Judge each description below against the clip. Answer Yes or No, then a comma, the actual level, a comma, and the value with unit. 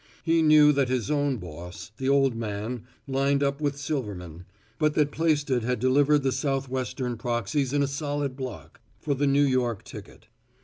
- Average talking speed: Yes, average, 175 wpm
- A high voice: No, low, 135 Hz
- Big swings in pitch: No, average, 2.9 semitones